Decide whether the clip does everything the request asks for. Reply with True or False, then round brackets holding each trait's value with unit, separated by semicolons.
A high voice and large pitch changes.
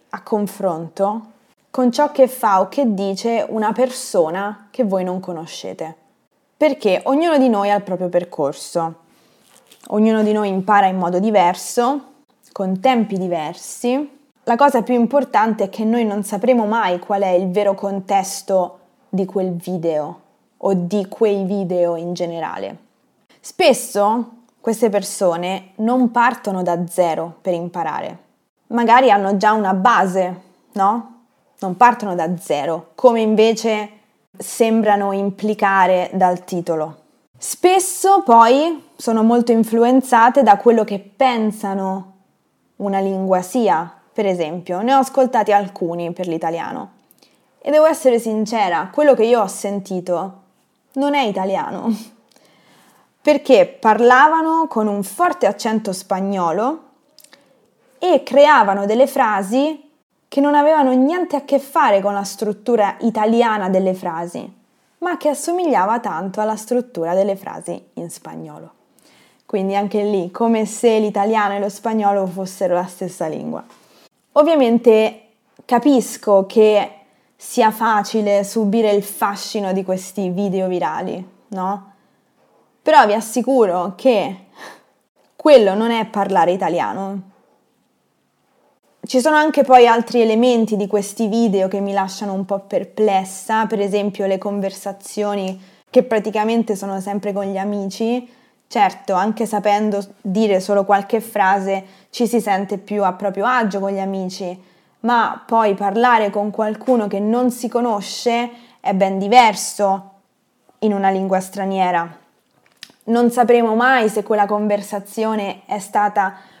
False (210 Hz; 3.8 semitones)